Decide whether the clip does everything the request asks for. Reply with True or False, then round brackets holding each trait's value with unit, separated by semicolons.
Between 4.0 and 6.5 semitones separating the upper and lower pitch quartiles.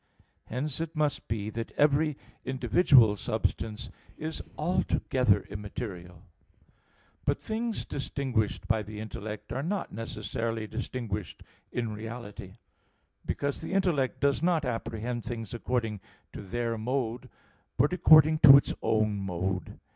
True (4.9 semitones)